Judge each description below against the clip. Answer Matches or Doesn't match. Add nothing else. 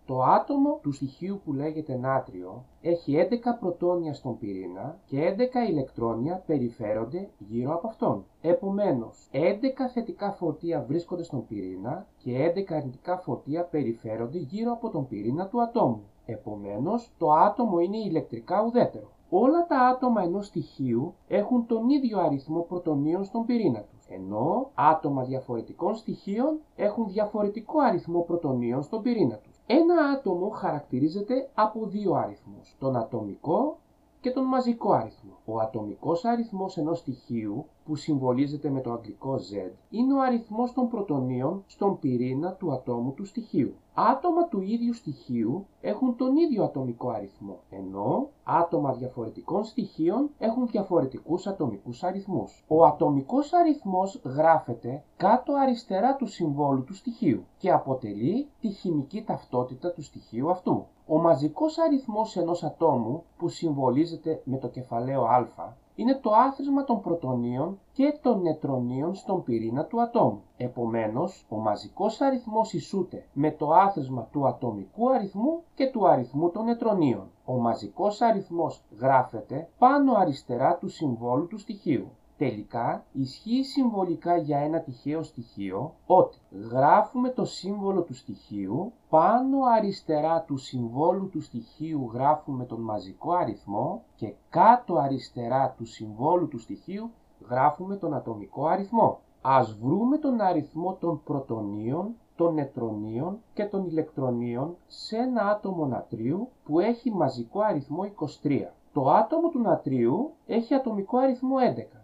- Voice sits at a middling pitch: Matches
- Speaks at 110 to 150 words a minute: Matches